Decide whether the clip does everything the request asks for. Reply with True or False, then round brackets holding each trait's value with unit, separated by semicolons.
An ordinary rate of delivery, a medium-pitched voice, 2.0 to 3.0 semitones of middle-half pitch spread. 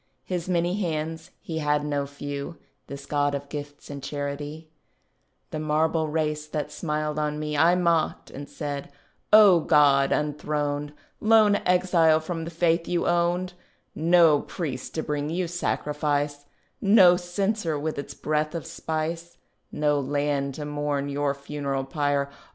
True (145 wpm; 150 Hz; 2.6 semitones)